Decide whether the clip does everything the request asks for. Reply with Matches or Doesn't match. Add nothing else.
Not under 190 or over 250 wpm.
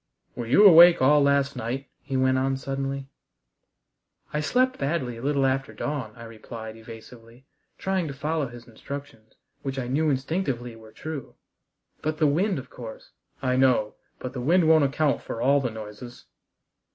Doesn't match